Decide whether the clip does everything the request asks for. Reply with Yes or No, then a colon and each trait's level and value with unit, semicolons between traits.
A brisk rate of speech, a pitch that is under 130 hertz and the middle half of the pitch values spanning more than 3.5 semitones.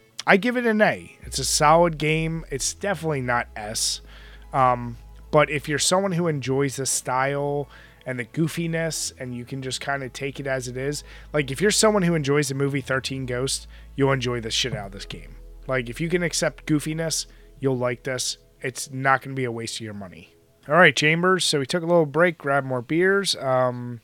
No: fast, 215 wpm; low, 135 Hz; average, 4.1 semitones